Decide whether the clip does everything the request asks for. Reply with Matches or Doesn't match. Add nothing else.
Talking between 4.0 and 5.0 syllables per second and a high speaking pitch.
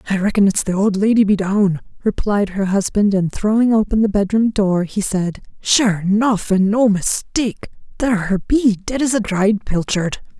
Matches